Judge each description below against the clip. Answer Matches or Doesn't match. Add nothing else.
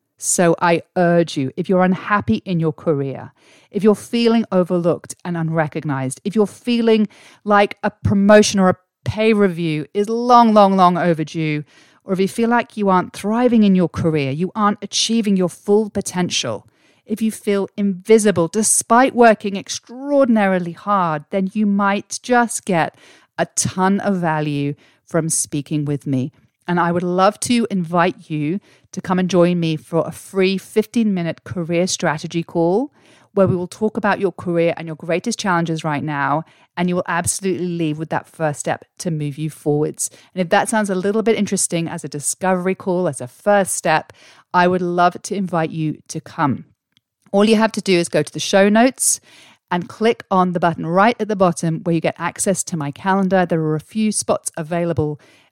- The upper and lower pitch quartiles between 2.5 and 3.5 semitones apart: Doesn't match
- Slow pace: Doesn't match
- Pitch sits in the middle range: Matches